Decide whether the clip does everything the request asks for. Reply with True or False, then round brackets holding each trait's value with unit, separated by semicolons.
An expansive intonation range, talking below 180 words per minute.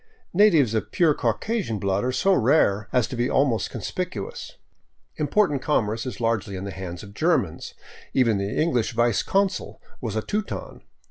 True (7.5 semitones; 160 wpm)